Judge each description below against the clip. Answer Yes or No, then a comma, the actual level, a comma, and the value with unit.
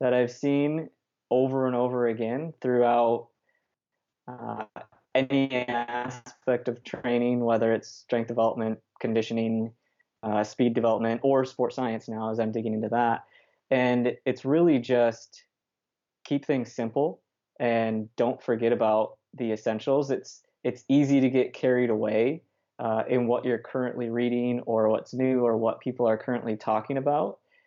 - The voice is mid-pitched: No, low, 120 Hz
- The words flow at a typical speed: Yes, average, 145 wpm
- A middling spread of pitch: No, narrow, 2.1 semitones